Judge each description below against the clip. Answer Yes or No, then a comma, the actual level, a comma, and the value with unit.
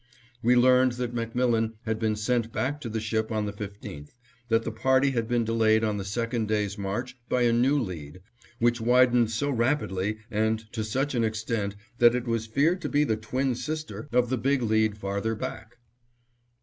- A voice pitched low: Yes, low, 115 Hz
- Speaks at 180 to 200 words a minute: Yes, average, 190 wpm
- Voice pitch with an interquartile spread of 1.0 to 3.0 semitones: Yes, narrow, 2.4 semitones